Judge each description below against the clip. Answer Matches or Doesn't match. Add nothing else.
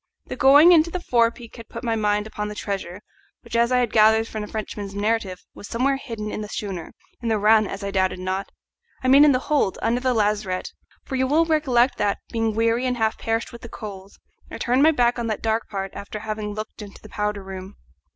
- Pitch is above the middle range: Matches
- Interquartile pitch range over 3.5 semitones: Doesn't match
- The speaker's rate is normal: Doesn't match